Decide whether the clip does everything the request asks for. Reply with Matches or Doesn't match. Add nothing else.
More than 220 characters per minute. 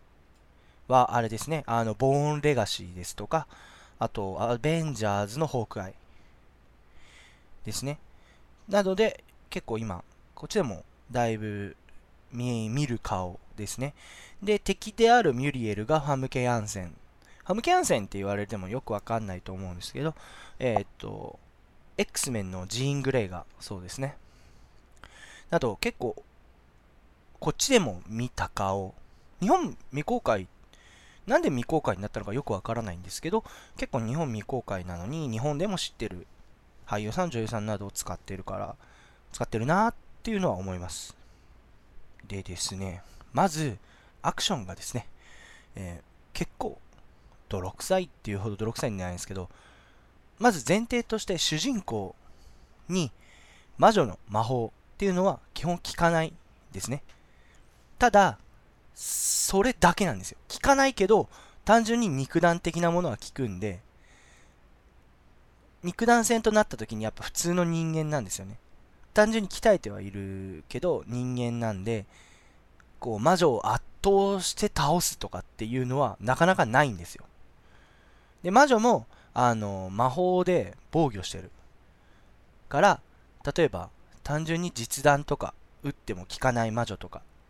Matches